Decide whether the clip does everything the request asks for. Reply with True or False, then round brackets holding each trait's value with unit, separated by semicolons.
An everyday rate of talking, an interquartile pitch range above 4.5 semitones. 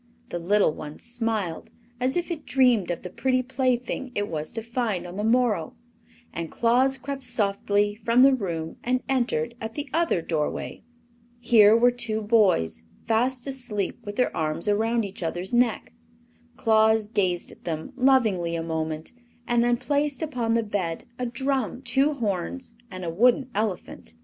True (165 wpm; 5.3 semitones)